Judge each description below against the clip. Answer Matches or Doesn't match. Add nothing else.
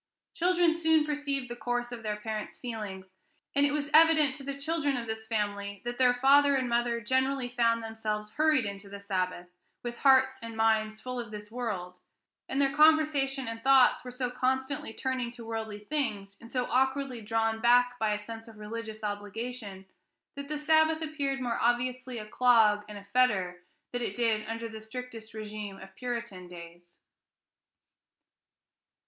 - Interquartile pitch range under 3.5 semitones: Doesn't match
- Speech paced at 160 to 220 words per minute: Matches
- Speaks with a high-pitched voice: Matches